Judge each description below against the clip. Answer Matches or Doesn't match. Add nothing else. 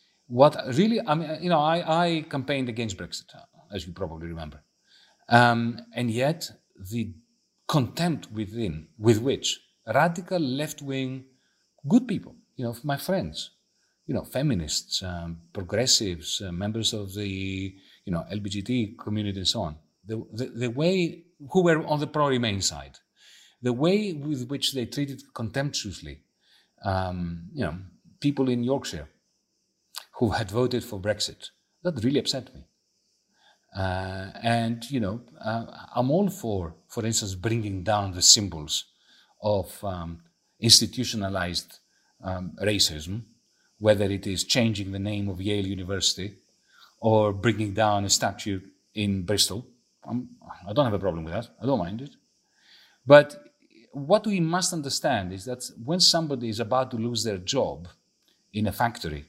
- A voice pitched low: Matches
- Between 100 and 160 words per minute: Matches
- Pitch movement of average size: Doesn't match